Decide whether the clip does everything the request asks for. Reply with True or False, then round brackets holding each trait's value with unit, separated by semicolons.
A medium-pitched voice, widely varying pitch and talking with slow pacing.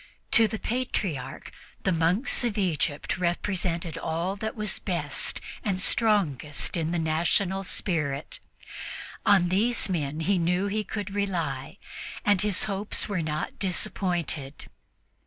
False (180 Hz; 4.0 semitones; 125 wpm)